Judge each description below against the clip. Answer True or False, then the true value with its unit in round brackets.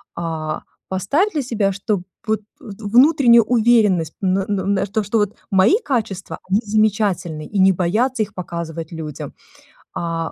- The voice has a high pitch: True (200 Hz)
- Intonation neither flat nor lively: True (4.2 semitones)